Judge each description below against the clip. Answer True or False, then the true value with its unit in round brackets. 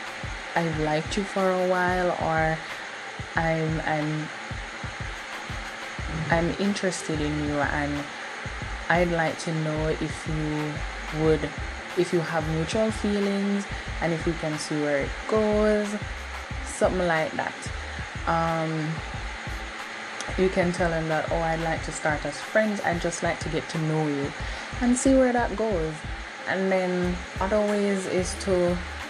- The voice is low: False (165 Hz)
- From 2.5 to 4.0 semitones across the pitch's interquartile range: True (3.3 semitones)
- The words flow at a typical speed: True (145 wpm)